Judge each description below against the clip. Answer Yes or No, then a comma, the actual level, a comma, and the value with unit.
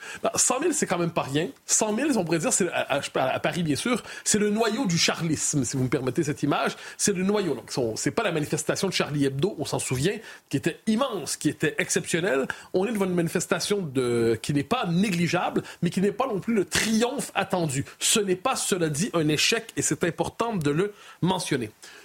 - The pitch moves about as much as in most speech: Yes, average, 5.0 semitones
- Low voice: No, medium, 180 Hz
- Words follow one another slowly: No, average, 215 wpm